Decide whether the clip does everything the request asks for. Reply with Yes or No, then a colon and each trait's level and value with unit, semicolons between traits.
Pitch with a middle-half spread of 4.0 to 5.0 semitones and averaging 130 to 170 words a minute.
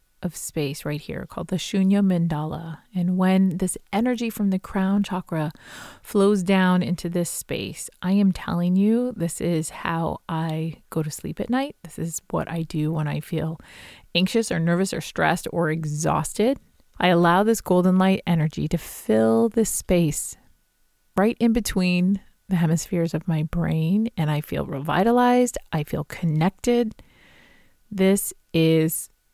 No: average, 3.6 semitones; average, 155 wpm